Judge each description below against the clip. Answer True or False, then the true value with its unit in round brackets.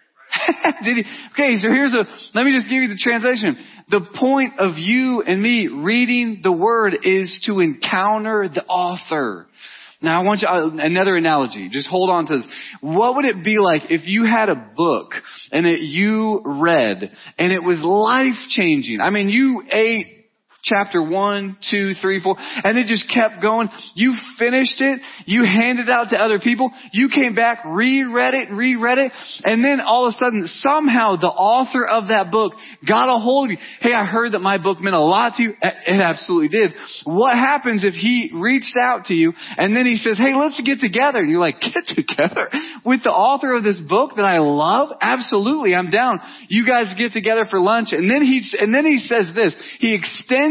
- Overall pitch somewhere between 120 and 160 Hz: False (230 Hz)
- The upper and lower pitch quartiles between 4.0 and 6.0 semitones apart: True (4.5 semitones)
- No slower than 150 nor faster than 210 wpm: True (200 wpm)